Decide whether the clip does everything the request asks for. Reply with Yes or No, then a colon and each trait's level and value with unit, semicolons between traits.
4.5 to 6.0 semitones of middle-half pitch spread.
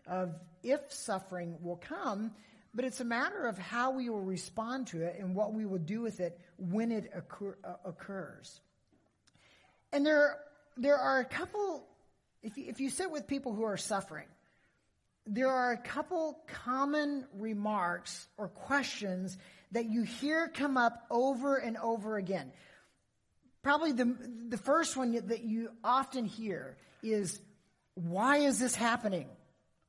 Yes: wide, 5.6 semitones